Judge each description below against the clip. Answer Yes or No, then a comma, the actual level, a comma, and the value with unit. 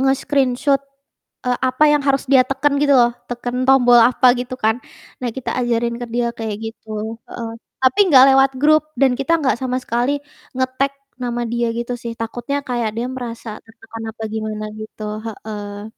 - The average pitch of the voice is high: Yes, high, 245 Hz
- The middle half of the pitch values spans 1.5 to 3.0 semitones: Yes, average, 2.7 semitones